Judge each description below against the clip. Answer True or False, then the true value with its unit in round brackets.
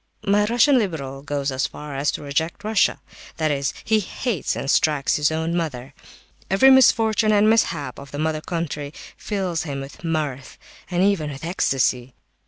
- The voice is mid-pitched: True (160 Hz)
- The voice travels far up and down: True (6.2 semitones)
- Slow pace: False (170 wpm)